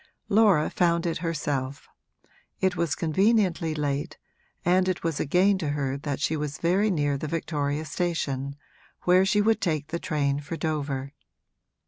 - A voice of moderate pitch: Yes, medium, 160 Hz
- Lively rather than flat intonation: No, average, 3.7 semitones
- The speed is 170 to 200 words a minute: No, average, 155 wpm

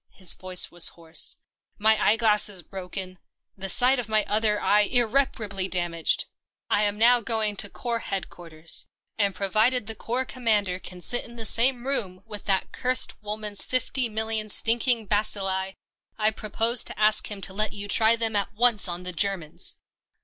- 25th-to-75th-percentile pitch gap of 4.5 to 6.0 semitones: No, average, 3.0 semitones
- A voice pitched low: No, high, 210 Hz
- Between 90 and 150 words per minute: No, average, 180 wpm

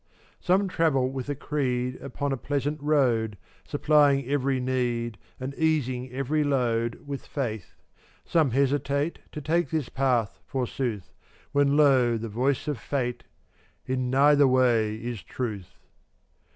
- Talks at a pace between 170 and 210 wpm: No, slow, 135 wpm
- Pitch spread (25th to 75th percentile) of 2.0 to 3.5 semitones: Yes, average, 2.8 semitones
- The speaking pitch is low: Yes, low, 130 Hz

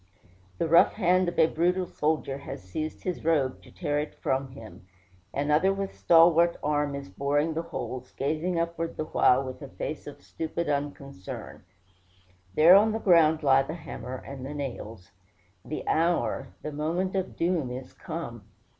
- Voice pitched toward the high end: No, medium, 155 Hz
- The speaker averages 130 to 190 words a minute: Yes, average, 165 wpm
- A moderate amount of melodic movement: Yes, average, 3.7 semitones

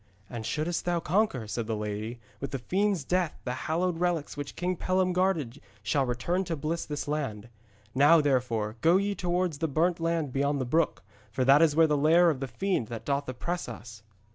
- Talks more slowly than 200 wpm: No, fast, 205 wpm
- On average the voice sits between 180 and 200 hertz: No, medium, 150 Hz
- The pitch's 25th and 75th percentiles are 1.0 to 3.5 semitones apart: No, wide, 5.6 semitones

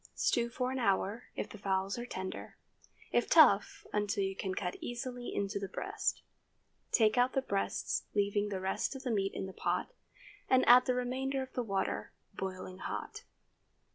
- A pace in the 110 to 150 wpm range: No, average, 170 wpm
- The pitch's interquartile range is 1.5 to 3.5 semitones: No, average, 4.4 semitones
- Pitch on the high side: Yes, high, 215 Hz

